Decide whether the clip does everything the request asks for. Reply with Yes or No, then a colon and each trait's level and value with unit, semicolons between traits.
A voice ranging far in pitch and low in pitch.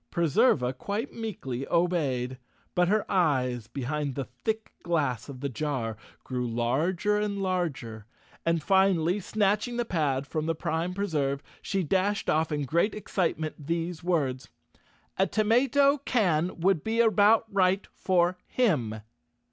No: wide, 6.3 semitones; medium, 170 Hz